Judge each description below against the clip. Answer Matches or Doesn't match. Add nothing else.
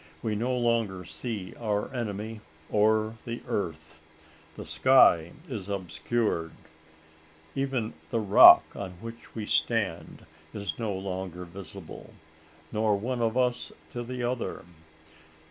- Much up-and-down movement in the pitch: Doesn't match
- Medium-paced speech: Doesn't match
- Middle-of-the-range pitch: Doesn't match